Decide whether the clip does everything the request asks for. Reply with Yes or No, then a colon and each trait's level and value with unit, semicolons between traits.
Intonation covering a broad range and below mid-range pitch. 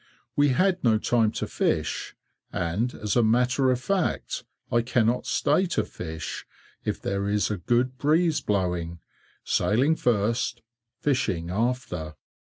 No: average, 4.6 semitones; low, 120 Hz